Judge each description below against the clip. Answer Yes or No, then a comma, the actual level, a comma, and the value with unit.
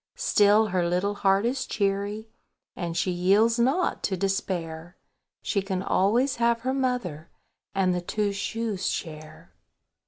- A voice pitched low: No, high, 200 Hz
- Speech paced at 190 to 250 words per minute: No, slow, 135 wpm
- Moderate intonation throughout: Yes, average, 4.1 semitones